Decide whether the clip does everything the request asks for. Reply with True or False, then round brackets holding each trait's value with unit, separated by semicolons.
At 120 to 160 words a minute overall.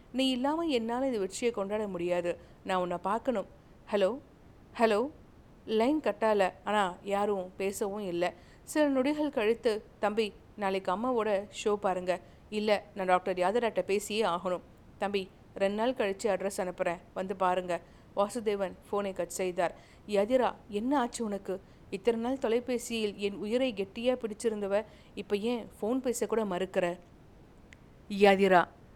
True (125 wpm)